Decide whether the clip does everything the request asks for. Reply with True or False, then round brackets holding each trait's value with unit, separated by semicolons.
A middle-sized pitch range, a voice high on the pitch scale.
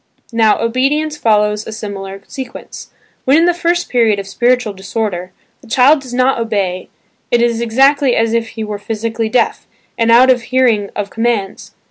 True (3.3 semitones; 230 Hz)